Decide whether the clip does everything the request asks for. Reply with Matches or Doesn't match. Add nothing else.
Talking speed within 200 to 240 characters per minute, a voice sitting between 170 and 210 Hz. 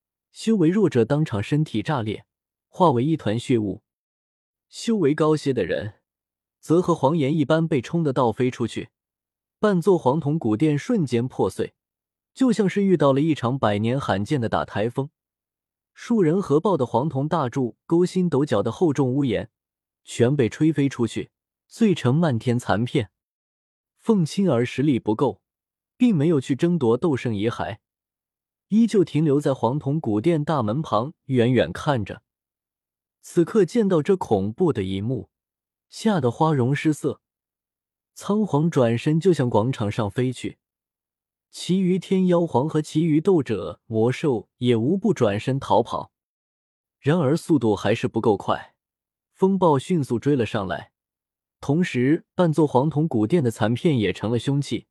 Doesn't match